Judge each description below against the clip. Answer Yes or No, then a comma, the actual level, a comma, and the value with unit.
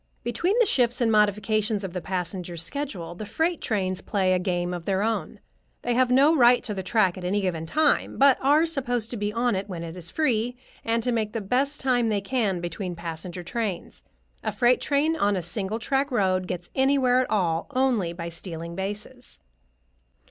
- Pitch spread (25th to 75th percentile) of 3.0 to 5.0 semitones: No, wide, 5.5 semitones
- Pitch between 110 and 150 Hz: No, high, 210 Hz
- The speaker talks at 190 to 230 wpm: Yes, average, 200 wpm